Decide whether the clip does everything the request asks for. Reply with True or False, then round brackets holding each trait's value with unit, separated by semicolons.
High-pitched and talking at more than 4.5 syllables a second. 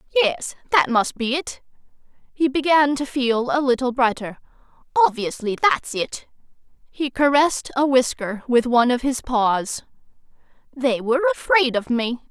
True (260 Hz; 4.8 syllables/s)